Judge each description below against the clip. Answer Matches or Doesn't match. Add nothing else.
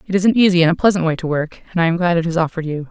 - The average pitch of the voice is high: Doesn't match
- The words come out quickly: Matches